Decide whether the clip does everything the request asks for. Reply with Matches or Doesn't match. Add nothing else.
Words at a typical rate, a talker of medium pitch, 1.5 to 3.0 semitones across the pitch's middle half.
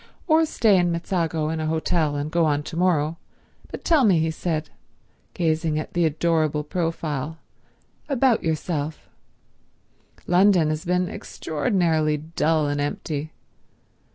Doesn't match